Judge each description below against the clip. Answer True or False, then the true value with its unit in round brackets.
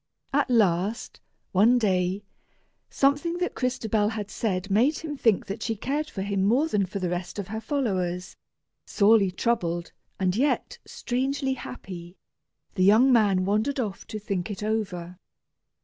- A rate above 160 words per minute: False (150 wpm)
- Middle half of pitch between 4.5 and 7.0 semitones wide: True (5.0 semitones)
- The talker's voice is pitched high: True (210 Hz)